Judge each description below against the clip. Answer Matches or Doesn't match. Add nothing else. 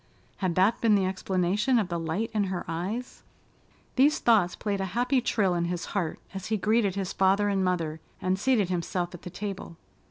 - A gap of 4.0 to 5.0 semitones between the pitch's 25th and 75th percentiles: Doesn't match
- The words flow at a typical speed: Matches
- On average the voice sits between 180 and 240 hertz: Matches